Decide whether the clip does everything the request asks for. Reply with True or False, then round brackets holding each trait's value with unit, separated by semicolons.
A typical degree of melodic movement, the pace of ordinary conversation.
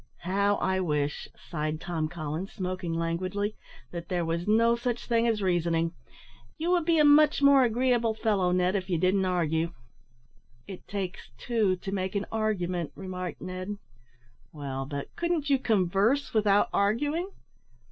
True (4.8 semitones; 150 wpm)